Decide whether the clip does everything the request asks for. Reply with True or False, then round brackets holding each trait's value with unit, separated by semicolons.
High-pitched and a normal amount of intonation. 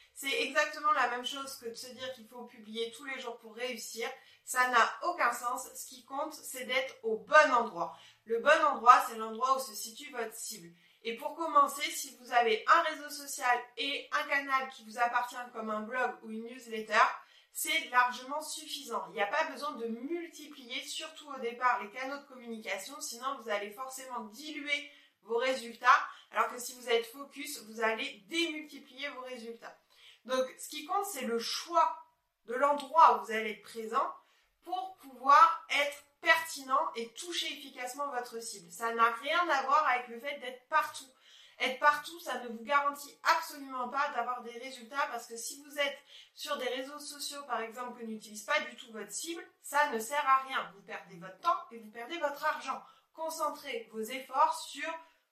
True (260 Hz; 4.0 semitones)